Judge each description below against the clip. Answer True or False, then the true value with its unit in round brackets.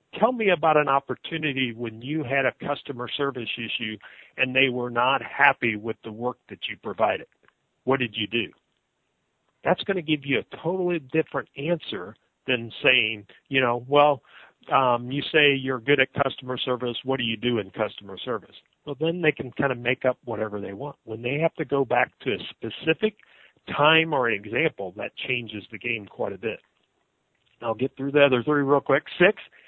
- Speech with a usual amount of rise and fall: True (3.6 semitones)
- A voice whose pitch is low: True (130 Hz)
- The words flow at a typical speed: True (190 wpm)